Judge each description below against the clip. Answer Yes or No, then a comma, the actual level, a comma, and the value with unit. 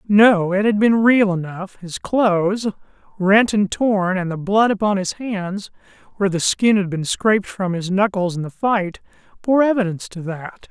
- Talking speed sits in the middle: Yes, average, 185 wpm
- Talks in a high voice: Yes, high, 200 Hz